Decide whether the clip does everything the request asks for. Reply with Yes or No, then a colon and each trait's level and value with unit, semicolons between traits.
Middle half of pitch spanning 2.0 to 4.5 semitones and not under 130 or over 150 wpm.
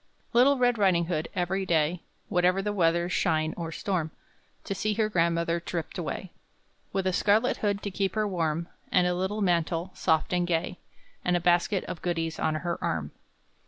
No: average, 2.7 semitones; average, 180 wpm